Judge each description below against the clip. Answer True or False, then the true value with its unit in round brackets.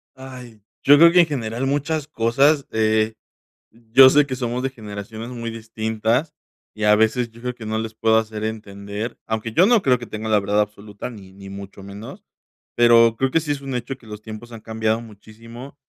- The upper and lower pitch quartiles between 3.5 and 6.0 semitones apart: False (2.9 semitones)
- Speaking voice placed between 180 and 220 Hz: False (115 Hz)